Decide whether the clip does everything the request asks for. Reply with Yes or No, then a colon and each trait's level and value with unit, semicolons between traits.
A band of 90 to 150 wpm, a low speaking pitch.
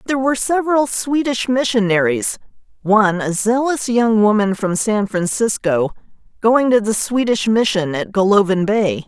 No: average, 140 wpm; high, 220 Hz